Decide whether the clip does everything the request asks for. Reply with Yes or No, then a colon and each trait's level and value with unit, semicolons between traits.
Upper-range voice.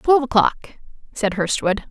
Yes: high, 230 Hz